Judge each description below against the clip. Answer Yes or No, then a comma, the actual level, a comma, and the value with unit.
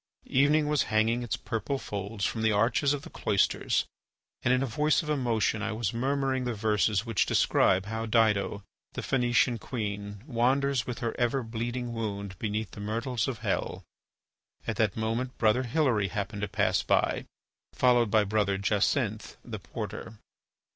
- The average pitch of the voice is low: Yes, low, 115 Hz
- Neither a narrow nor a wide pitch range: Yes, average, 3.1 semitones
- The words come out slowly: No, average, 160 wpm